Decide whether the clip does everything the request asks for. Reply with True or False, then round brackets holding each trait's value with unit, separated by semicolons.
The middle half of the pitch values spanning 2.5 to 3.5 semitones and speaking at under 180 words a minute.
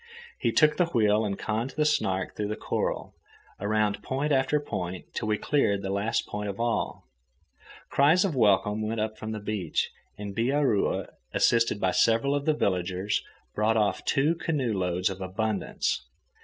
False (5.1 semitones; 170 wpm)